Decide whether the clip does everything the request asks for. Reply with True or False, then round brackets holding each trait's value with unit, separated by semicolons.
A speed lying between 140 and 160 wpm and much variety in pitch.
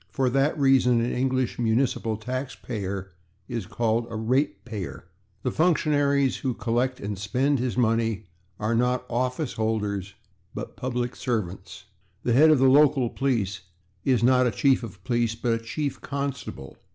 False (150 wpm; 3.1 semitones)